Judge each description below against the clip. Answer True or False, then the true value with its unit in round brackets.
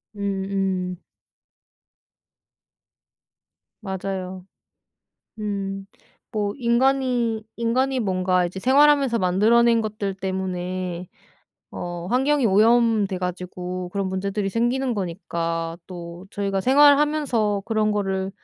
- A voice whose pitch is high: True (200 Hz)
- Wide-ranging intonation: False (4.2 semitones)